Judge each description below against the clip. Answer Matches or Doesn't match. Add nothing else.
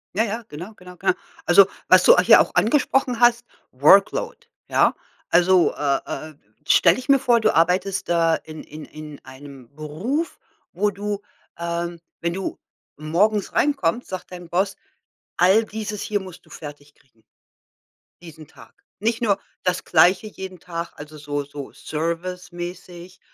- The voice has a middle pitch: Matches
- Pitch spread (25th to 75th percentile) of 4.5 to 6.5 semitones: Matches